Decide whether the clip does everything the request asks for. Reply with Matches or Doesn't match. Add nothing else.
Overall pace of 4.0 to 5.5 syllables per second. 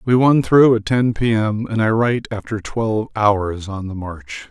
Matches